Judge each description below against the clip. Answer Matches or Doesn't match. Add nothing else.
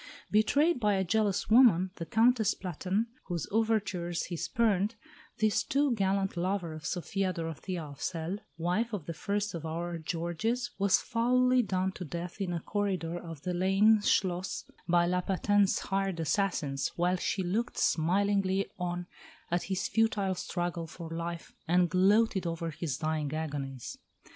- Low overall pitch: Doesn't match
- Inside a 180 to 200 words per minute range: Doesn't match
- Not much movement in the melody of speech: Doesn't match